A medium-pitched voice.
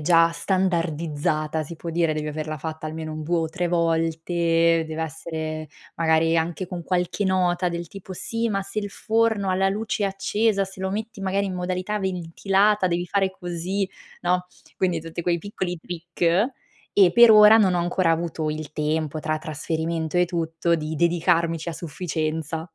Yes: medium, 170 Hz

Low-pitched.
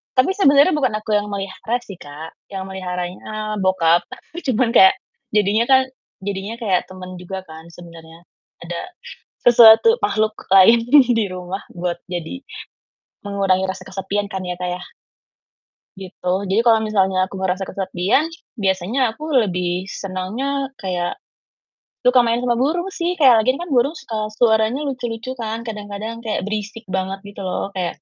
No: high, 200 Hz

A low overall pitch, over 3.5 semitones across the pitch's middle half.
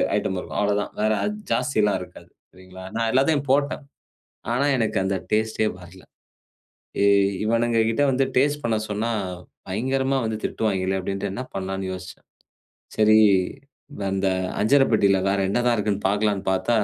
Yes: low, 110 Hz; average, 3.9 semitones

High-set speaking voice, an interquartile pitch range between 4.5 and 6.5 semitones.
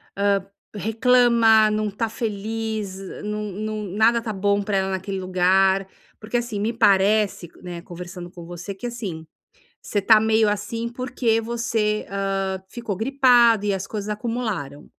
No: high, 210 Hz; average, 2.8 semitones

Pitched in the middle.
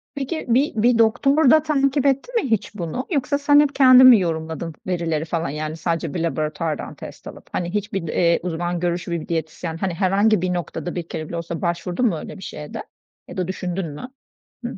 Yes: medium, 180 Hz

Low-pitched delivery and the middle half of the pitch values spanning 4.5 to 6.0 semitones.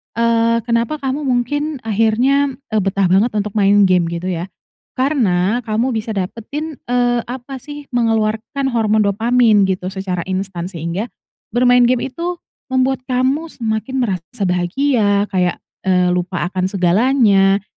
No: high, 225 Hz; average, 4.8 semitones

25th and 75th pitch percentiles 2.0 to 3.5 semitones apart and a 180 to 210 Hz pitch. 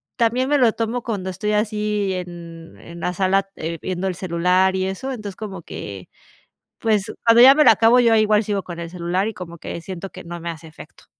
No: average, 4.1 semitones; high, 190 Hz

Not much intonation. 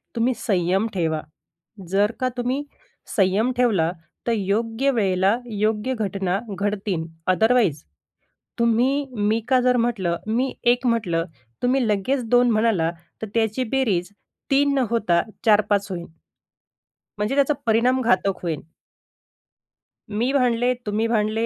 No: average, 4.0 semitones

